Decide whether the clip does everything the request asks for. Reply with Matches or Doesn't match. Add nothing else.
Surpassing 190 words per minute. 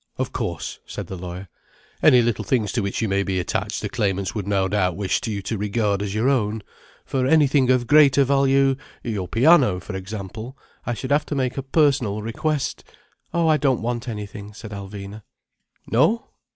Doesn't match